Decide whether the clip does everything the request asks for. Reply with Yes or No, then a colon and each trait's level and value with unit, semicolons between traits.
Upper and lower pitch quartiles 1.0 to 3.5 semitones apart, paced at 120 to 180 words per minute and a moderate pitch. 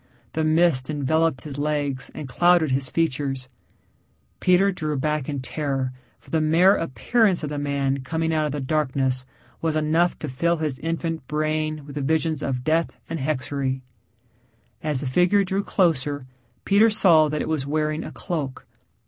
Yes: average, 3.1 semitones; average, 165 wpm; medium, 155 Hz